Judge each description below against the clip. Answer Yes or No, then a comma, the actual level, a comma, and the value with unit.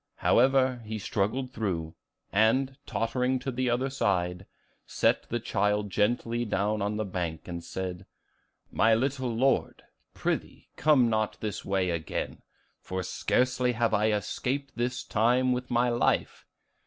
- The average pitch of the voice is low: Yes, low, 115 Hz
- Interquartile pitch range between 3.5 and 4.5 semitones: Yes, average, 3.9 semitones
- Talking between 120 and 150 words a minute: Yes, slow, 135 wpm